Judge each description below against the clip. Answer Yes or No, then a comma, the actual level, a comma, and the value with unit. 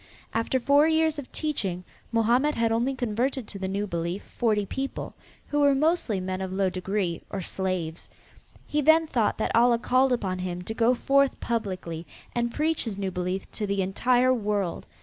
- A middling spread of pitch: No, wide, 5.7 semitones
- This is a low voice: No, high, 225 Hz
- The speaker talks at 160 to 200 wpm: Yes, average, 180 wpm